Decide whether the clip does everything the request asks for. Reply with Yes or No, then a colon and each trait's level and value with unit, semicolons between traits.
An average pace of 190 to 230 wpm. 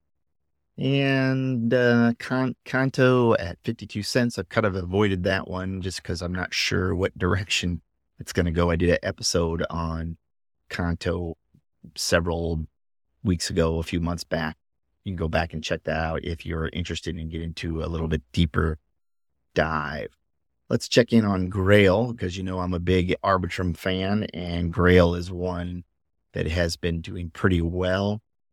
No: average, 165 wpm